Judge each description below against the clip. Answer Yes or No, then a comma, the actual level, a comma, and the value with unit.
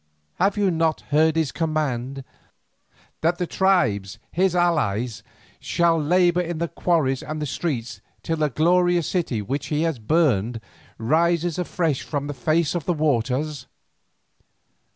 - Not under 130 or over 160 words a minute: Yes, average, 140 wpm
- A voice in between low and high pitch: Yes, medium, 155 Hz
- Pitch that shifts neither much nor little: Yes, average, 4.1 semitones